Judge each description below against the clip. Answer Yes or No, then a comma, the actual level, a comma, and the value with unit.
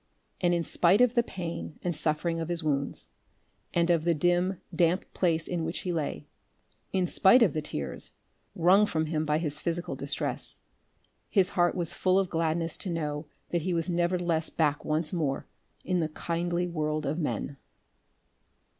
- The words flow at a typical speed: Yes, average, 170 wpm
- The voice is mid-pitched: Yes, medium, 170 Hz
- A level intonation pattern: Yes, narrow, 2.1 semitones